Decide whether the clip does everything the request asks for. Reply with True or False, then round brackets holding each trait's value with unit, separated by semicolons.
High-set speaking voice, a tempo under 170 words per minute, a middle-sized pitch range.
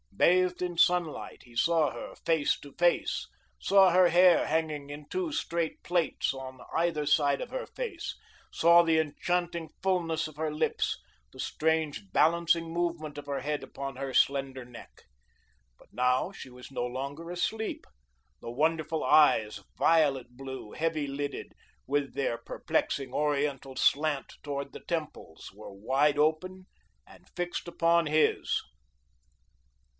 False (155 Hz; 140 wpm; 3.7 semitones)